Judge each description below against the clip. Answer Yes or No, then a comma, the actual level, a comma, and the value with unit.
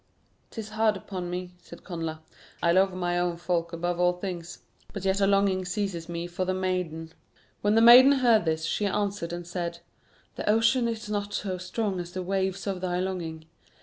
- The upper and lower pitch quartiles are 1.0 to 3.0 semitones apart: Yes, average, 2.7 semitones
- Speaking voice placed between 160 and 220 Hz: Yes, medium, 185 Hz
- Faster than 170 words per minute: Yes, average, 190 wpm